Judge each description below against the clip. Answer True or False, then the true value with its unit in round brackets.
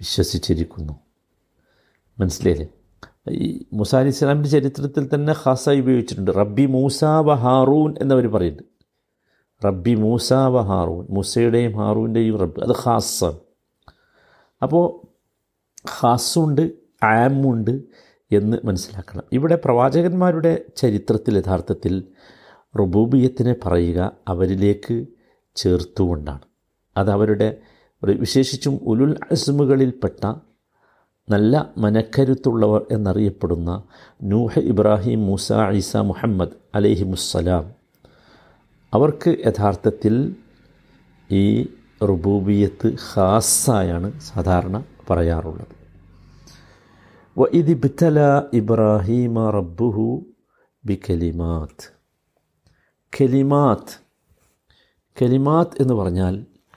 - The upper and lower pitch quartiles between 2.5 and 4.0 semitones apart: False (5.3 semitones)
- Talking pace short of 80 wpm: True (65 wpm)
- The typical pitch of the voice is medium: False (110 Hz)